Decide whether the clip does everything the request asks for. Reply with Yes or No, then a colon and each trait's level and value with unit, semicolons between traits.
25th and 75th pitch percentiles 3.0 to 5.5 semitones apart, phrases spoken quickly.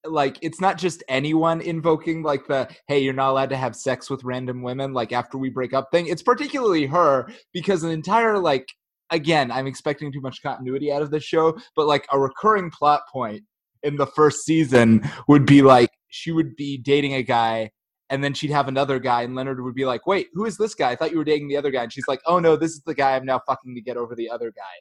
Yes: average, 3.7 semitones; fast, 245 wpm